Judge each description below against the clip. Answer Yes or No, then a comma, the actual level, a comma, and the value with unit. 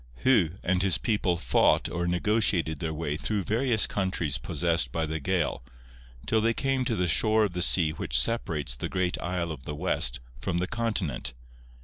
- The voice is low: Yes, very low, 90 Hz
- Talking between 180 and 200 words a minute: Yes, average, 185 wpm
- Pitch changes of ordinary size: Yes, average, 5.0 semitones